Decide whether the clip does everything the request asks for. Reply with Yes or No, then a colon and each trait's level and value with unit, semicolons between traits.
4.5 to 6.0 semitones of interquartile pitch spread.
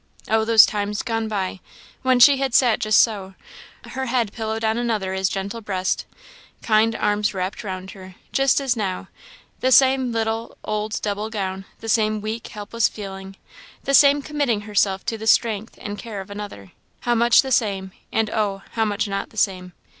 No: average, 2.7 semitones